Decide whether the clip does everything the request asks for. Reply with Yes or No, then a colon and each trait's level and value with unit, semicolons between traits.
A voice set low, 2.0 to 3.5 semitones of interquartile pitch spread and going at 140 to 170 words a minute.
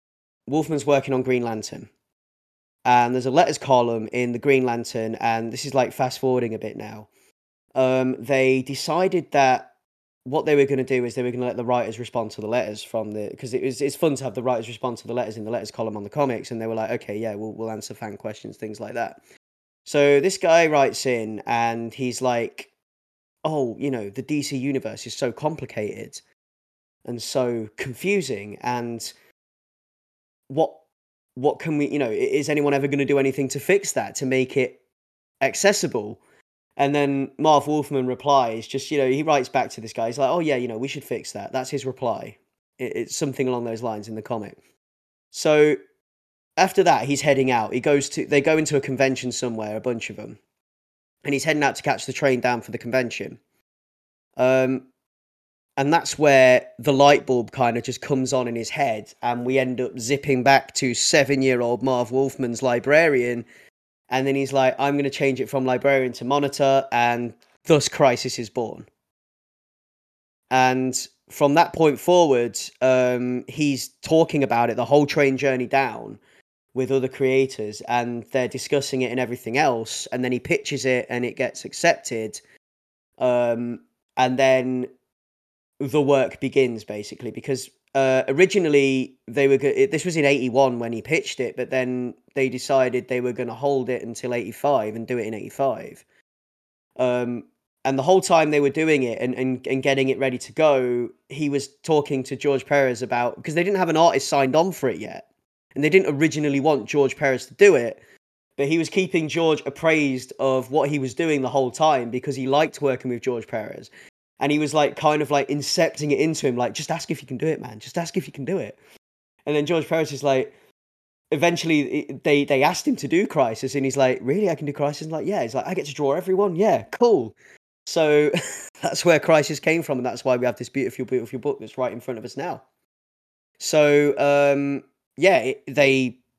No: low, 130 Hz; average, 3.0 semitones; fast, 205 wpm